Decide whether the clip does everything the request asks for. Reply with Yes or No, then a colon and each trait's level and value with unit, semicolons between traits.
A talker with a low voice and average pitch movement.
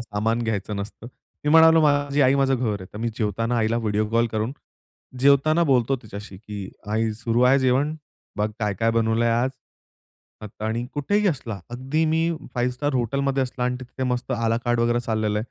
Yes: low, 120 Hz; average, 3.5 semitones